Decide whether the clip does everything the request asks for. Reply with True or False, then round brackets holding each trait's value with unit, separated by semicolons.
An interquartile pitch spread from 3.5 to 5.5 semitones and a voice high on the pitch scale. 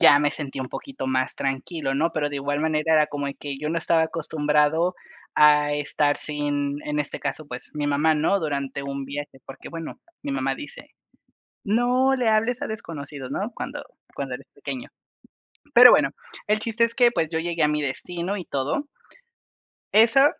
False (4.7 semitones; 150 Hz)